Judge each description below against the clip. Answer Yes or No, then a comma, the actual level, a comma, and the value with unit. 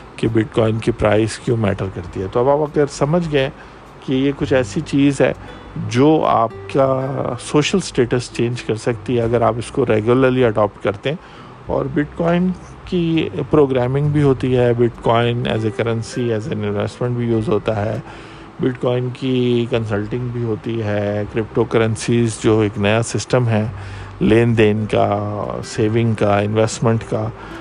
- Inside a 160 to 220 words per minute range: Yes, average, 170 wpm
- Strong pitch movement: No, average, 3.2 semitones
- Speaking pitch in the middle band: No, low, 120 Hz